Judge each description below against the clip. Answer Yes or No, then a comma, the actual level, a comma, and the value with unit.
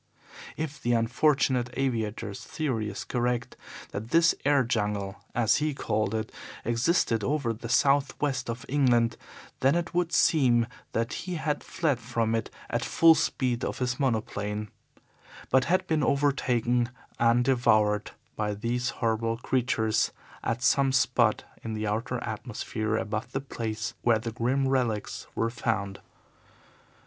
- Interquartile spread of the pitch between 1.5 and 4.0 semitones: Yes, average, 3.4 semitones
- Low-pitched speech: Yes, low, 120 Hz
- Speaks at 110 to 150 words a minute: Yes, average, 145 wpm